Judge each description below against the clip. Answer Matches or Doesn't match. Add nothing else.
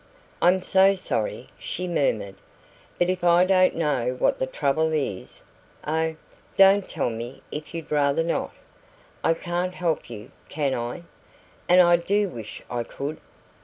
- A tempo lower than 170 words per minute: Matches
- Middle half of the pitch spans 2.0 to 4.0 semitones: Doesn't match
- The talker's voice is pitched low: Doesn't match